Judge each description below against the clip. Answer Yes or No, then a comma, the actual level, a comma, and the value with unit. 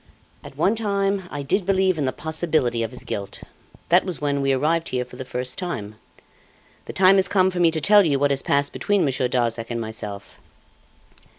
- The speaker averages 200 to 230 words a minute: Yes, fast, 205 wpm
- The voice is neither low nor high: Yes, medium, 145 Hz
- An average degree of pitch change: No, wide, 6.9 semitones